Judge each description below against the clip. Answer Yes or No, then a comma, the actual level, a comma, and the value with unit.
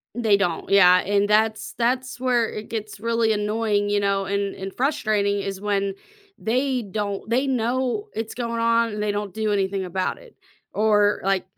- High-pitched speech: Yes, high, 210 Hz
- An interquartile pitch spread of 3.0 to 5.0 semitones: No, narrow, 2.5 semitones